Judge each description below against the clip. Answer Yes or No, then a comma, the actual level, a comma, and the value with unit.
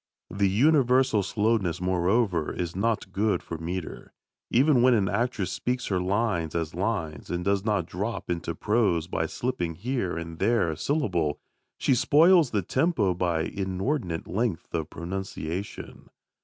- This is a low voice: Yes, very low, 95 Hz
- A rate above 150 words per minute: No, average, 145 wpm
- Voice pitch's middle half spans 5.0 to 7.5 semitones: Yes, average, 5.3 semitones